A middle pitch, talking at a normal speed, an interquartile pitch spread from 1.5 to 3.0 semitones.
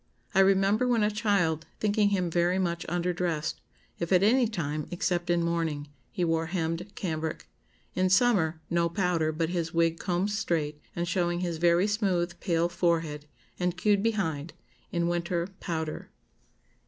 Yes: medium, 175 Hz; average, 155 wpm; narrow, 2.6 semitones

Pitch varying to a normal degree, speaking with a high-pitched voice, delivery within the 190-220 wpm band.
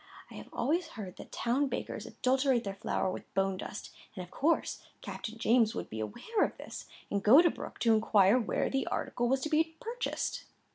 No: wide, 6.8 semitones; high, 240 Hz; average, 200 wpm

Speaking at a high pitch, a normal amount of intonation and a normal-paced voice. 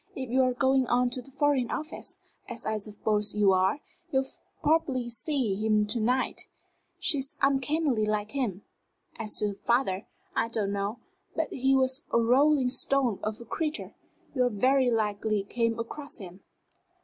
Yes: high, 245 Hz; average, 4.0 semitones; average, 160 wpm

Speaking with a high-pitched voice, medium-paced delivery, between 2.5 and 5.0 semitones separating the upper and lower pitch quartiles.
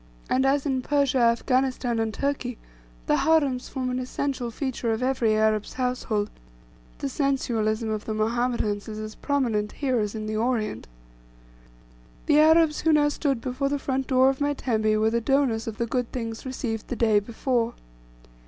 Yes: very high, 250 Hz; average, 170 wpm; average, 3.5 semitones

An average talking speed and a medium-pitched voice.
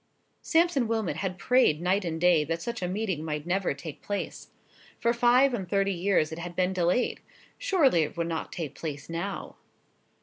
Yes: average, 180 wpm; medium, 180 Hz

